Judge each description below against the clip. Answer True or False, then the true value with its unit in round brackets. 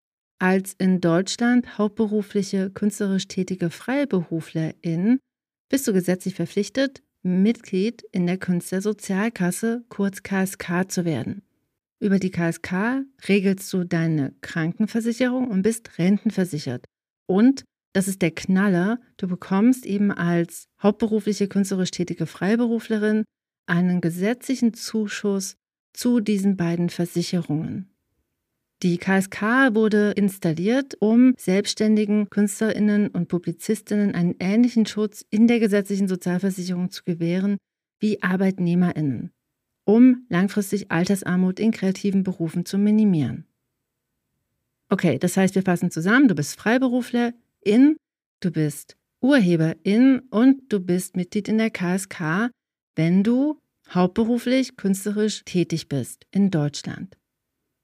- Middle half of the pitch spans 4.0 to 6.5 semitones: False (3.6 semitones)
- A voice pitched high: True (200 Hz)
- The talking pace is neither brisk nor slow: False (110 wpm)